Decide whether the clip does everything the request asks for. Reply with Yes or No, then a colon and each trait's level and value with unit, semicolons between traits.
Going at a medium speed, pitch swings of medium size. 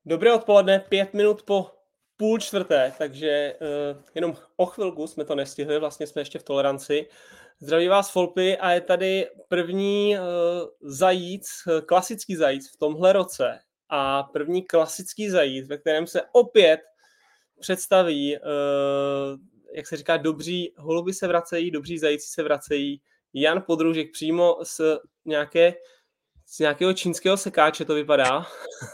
Yes: average, 135 wpm; average, 4.1 semitones